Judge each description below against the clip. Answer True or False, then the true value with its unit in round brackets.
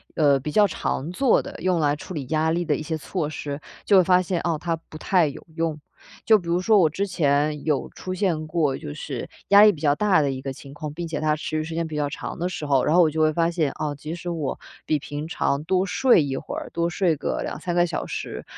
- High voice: False (160 Hz)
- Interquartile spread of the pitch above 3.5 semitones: False (3.0 semitones)